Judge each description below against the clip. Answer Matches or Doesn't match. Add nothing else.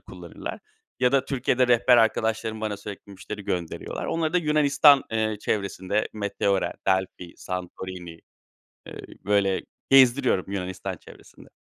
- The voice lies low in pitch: Matches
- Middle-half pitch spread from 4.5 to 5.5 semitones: Matches